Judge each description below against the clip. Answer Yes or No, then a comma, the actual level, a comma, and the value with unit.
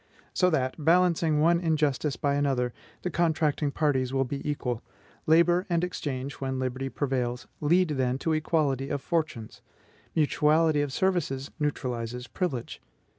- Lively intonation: No, average, 3.6 semitones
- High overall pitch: No, medium, 145 Hz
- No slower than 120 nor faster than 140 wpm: Yes, slow, 135 wpm